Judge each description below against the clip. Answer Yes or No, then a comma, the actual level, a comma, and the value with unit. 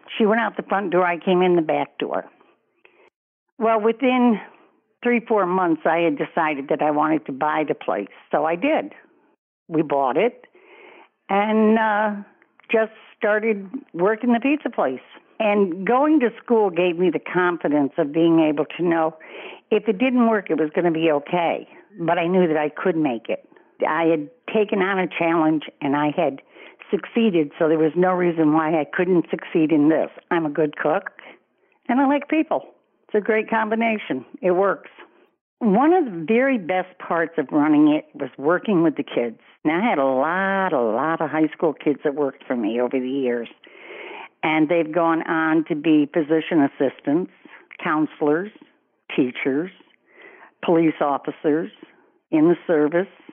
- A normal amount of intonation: No, wide, 6.0 semitones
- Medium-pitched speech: Yes, medium, 180 Hz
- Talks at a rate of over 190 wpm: No, average, 175 wpm